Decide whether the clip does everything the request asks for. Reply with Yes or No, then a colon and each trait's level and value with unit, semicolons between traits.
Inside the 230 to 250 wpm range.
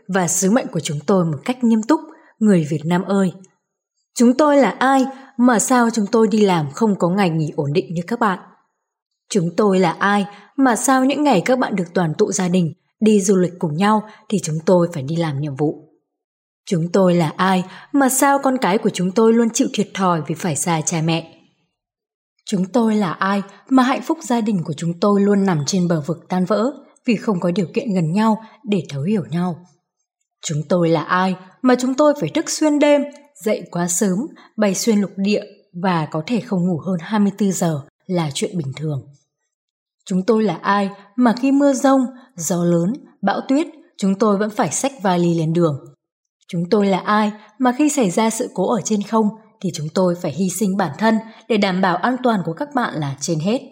No: average, 215 wpm